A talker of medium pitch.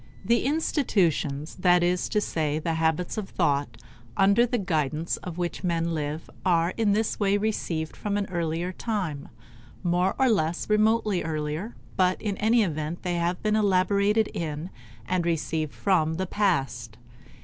Yes: medium, 180 Hz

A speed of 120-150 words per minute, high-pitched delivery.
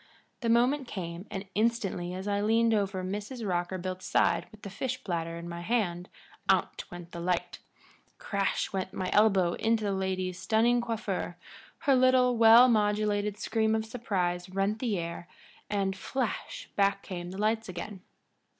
No: average, 160 wpm; high, 200 Hz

